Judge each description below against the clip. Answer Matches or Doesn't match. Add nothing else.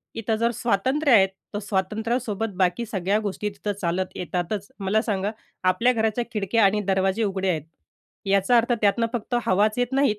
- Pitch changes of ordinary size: Matches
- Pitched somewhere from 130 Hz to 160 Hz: Doesn't match